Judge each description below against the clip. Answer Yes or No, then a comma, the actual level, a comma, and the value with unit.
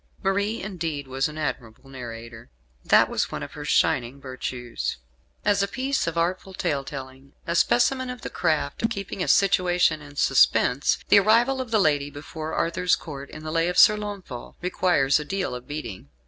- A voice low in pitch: No, medium, 155 Hz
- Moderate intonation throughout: No, wide, 6.4 semitones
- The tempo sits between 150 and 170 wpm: No, average, 185 wpm